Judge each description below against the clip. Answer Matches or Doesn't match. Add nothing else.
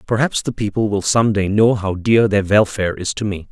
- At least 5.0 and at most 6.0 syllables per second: Matches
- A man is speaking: Matches